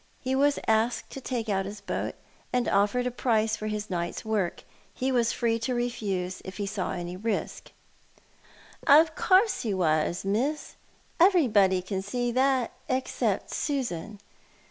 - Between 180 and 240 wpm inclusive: No, average, 155 wpm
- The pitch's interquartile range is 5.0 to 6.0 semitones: No, average, 4.6 semitones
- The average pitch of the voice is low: No, high, 225 Hz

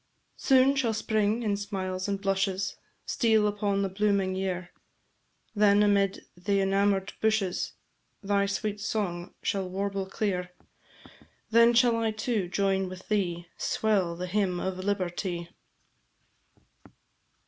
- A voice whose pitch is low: No, high, 200 Hz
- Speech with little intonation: Yes, narrow, 2.1 semitones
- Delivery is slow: Yes, slow, 120 wpm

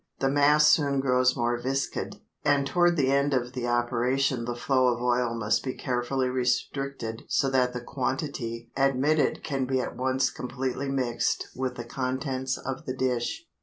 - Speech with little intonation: Yes, narrow, 1.9 semitones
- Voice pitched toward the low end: Yes, low, 130 Hz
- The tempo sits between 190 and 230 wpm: No, average, 165 wpm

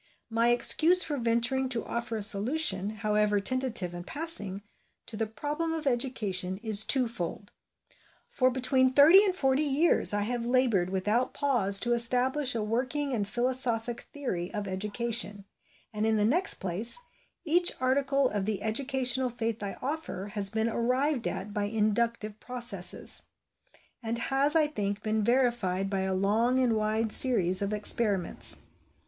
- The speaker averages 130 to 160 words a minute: Yes, average, 150 wpm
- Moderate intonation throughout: Yes, average, 4.0 semitones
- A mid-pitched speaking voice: No, high, 235 Hz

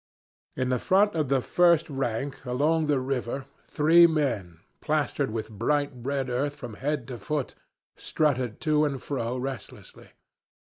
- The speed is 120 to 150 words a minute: Yes, average, 140 wpm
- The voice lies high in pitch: No, low, 135 Hz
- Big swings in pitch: No, average, 3.4 semitones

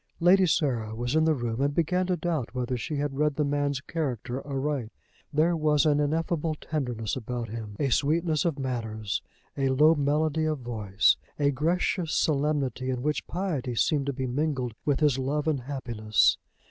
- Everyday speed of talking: Yes, average, 175 wpm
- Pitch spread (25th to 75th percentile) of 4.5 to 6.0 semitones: No, average, 3.8 semitones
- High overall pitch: No, medium, 140 Hz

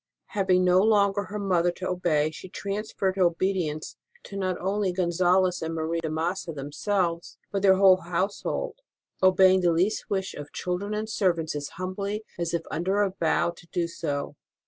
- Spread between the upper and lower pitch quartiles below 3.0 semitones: Yes, narrow, 2.6 semitones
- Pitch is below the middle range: No, medium, 185 Hz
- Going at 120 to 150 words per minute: No, average, 180 wpm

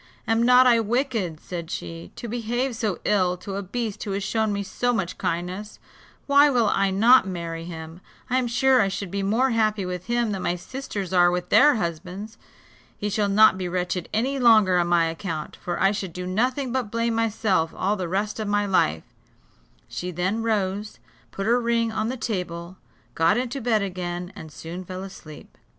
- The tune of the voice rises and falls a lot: No, average, 4.3 semitones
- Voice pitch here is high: Yes, high, 200 Hz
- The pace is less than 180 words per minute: No, average, 195 wpm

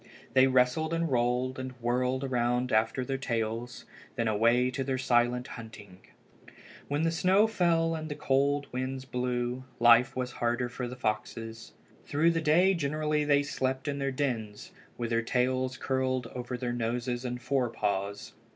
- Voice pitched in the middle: No, low, 125 Hz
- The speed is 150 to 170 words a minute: Yes, average, 160 wpm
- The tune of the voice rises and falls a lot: No, narrow, 2.6 semitones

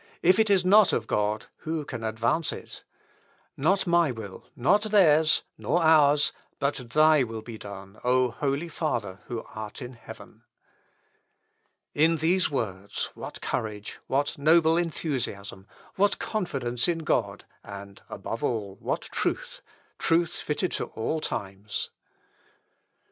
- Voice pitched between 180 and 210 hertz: No, medium, 140 Hz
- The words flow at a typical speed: No, slow, 130 wpm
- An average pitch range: No, wide, 6.9 semitones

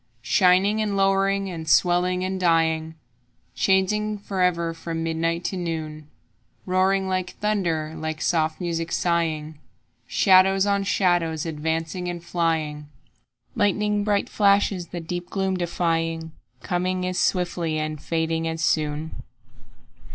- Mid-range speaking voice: Yes, medium, 175 Hz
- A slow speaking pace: Yes, slow, 120 wpm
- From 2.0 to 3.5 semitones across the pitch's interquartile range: Yes, average, 2.8 semitones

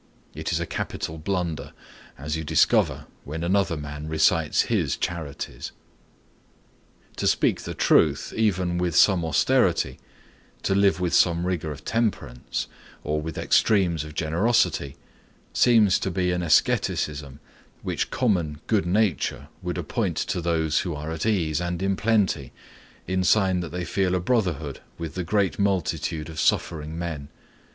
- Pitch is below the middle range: Yes, very low, 85 Hz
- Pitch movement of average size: Yes, average, 3.6 semitones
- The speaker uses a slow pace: No, average, 145 wpm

